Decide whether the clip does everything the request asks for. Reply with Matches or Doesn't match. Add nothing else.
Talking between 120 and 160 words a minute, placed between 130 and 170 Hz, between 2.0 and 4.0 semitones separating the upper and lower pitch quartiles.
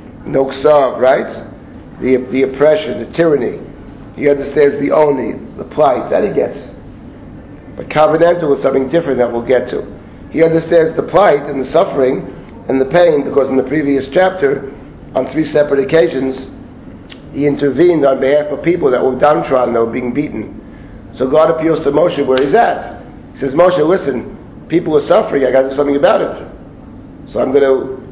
Doesn't match